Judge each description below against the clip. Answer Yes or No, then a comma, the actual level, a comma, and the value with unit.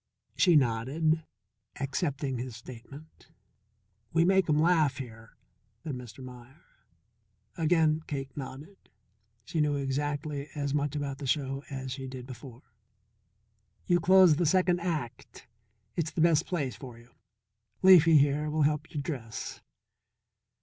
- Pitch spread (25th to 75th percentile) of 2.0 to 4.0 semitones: Yes, average, 3.3 semitones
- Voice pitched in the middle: Yes, medium, 145 Hz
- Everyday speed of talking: No, slow, 130 wpm